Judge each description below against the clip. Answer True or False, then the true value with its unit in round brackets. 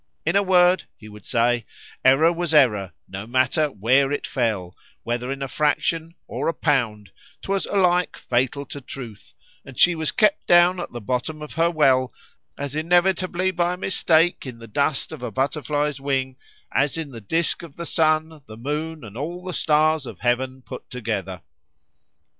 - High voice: False (145 Hz)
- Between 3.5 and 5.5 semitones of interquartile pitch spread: True (5.2 semitones)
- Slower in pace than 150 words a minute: False (165 wpm)